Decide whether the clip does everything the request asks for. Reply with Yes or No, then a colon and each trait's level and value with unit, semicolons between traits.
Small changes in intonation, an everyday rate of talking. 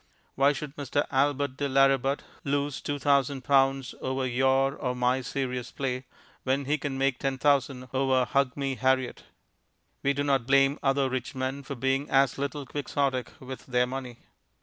Yes: narrow, 1.3 semitones; average, 170 wpm